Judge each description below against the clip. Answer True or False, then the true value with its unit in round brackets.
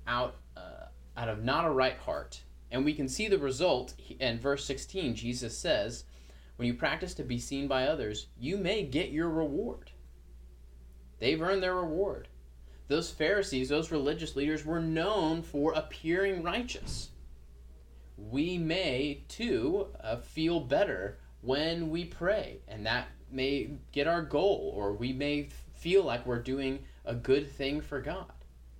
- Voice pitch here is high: False (140 Hz)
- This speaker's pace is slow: False (155 wpm)